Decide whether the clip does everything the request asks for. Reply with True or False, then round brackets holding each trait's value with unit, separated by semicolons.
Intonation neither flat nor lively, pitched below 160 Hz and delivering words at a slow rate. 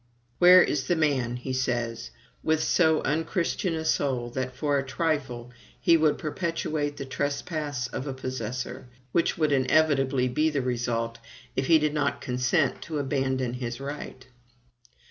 False (3.7 semitones; 140 Hz; 150 wpm)